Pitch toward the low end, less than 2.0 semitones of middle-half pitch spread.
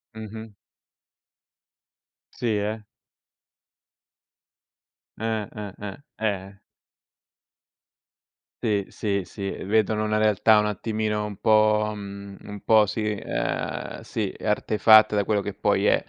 Yes: low, 105 Hz; narrow, 1.3 semitones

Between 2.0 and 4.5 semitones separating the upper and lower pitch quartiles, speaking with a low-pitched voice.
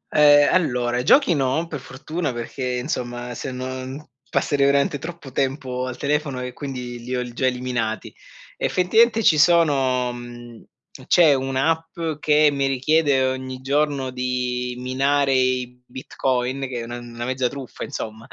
Yes: narrow, 2.6 semitones; low, 130 Hz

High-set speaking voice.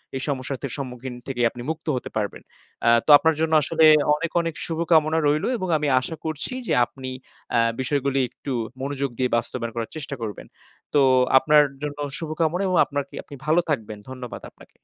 No: medium, 140 Hz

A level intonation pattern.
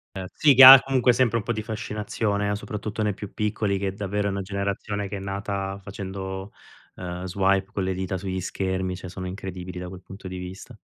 Yes: narrow, 1.8 semitones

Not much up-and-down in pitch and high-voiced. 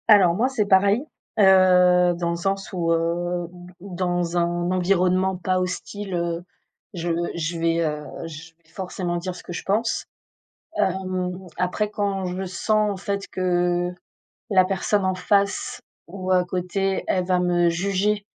No: narrow, 1.8 semitones; medium, 180 Hz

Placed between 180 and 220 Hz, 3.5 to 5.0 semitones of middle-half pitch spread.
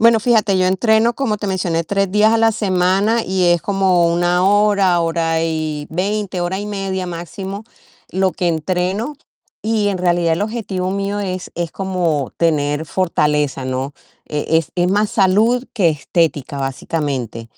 Yes: medium, 185 Hz; average, 3.8 semitones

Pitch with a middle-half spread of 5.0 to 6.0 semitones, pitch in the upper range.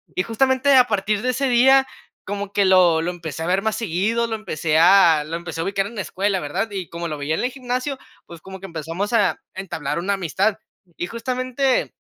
Yes: wide, 5.4 semitones; high, 195 Hz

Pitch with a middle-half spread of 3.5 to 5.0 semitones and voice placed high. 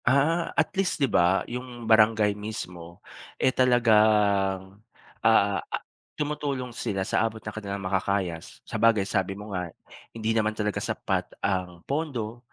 No: average, 3.9 semitones; low, 110 Hz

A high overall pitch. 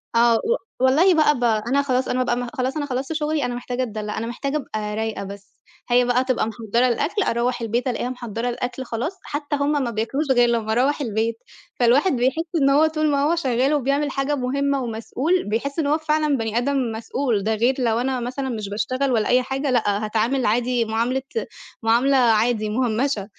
Yes: very high, 250 Hz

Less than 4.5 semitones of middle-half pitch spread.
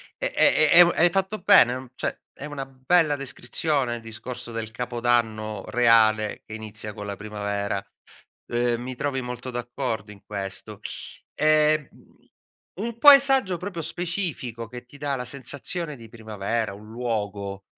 No: wide, 5.6 semitones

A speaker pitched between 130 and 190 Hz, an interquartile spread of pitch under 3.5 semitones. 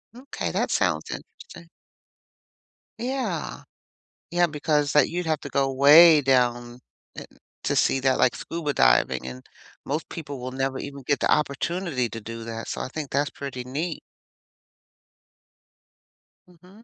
No: medium, 140 Hz; average, 4.5 semitones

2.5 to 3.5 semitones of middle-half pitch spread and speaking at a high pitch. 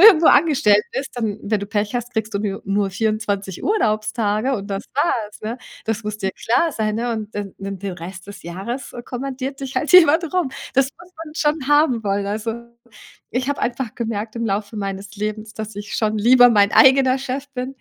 No: average, 4.4 semitones; high, 220 Hz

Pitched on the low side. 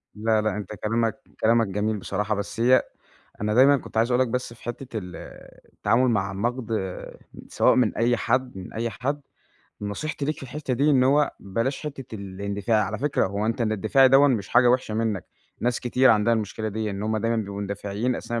Yes: low, 115 Hz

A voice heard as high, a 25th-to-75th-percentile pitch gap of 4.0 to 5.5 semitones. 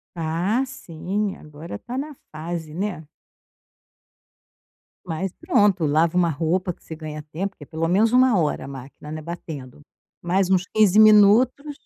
No: medium, 175 Hz; average, 4.7 semitones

